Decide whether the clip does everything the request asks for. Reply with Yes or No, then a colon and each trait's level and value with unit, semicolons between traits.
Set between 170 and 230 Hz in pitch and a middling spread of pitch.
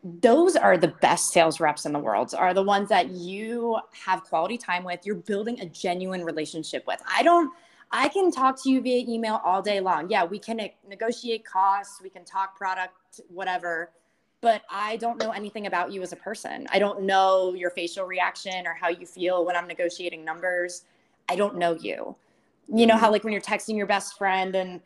Yes: high, 190 Hz; average, 3.6 semitones